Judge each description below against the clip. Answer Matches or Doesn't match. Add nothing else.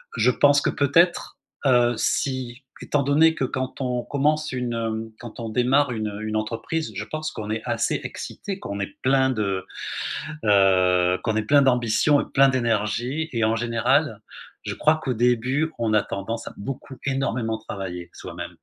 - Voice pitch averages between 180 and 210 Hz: Doesn't match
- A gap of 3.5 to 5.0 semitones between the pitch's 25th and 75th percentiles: Matches